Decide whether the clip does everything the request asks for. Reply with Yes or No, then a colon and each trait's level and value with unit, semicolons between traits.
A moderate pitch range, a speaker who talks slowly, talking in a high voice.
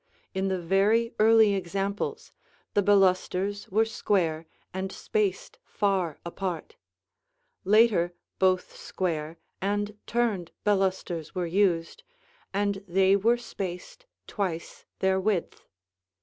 No: narrow, 2.3 semitones; slow, 105 wpm; high, 195 Hz